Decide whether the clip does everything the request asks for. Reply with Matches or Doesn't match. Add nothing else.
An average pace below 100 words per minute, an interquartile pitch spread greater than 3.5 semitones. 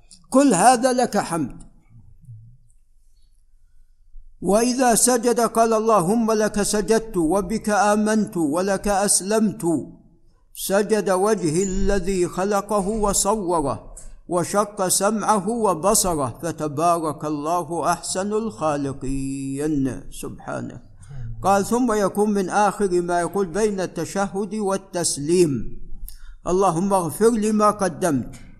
Matches